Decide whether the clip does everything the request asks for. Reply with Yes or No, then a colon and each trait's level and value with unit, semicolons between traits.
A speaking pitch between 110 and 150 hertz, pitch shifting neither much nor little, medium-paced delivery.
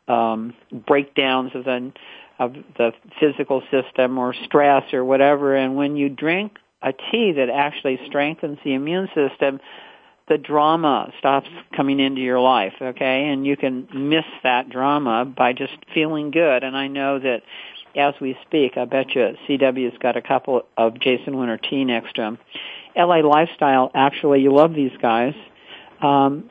No: low, 135 Hz; narrow, 2.2 semitones; average, 165 wpm